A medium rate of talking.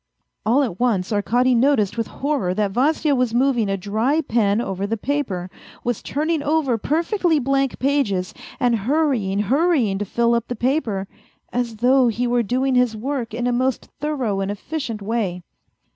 Yes: average, 175 wpm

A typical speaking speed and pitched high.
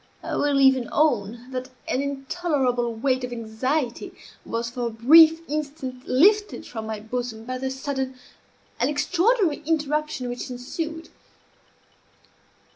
No: slow, 125 wpm; very high, 265 Hz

